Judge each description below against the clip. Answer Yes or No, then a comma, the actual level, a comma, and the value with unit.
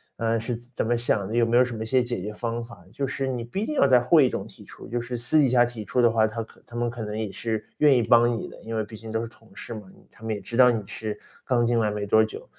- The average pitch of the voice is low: Yes, low, 115 Hz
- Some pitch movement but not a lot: No, narrow, 1.6 semitones